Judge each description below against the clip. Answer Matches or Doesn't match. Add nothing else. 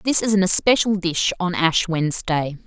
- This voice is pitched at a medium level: Matches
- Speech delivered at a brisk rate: Doesn't match